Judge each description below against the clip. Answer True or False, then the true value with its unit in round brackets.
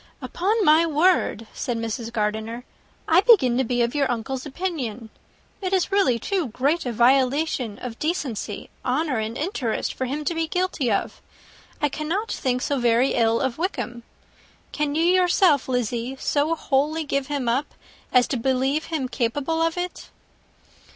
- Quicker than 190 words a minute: False (165 wpm)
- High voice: True (270 Hz)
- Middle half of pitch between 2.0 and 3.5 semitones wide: False (5.2 semitones)